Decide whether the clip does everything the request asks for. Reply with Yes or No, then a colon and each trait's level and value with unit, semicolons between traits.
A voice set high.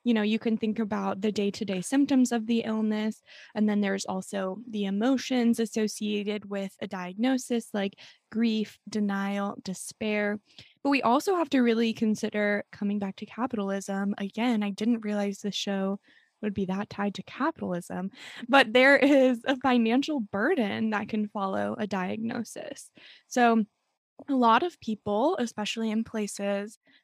Yes: high, 220 Hz